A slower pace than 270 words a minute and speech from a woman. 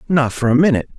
No: fast, 245 wpm; male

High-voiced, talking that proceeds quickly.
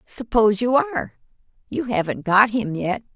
No: high, 220 Hz; average, 150 wpm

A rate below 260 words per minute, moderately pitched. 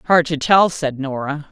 Yes: average, 200 wpm; medium, 155 Hz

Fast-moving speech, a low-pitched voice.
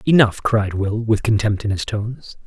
No: average, 195 wpm; low, 110 Hz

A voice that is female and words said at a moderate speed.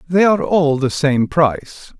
No: male; average, 180 wpm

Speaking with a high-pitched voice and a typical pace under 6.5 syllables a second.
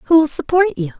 Yes: very high, 290 Hz; 4.4 syllables/s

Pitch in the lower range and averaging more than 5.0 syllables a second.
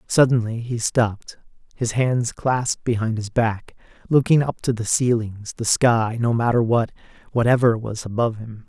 No: low, 115 Hz; 4.8 syllables/s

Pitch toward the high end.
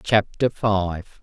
No: low, 100 Hz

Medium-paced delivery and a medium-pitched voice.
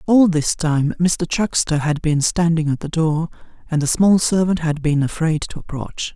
Yes: average, 195 wpm; medium, 160 Hz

